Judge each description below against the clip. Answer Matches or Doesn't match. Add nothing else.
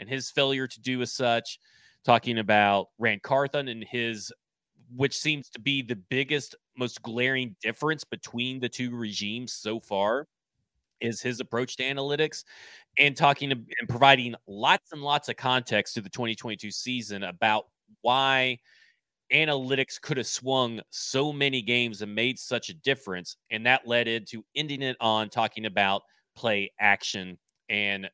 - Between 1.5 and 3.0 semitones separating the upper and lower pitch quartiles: Doesn't match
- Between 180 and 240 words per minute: Doesn't match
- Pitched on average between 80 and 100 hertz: Doesn't match